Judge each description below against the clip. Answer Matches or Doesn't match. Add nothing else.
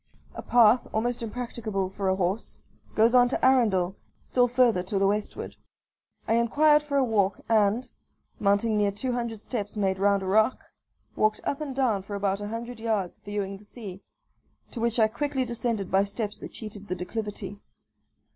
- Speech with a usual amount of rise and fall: Matches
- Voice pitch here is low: Doesn't match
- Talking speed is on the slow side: Doesn't match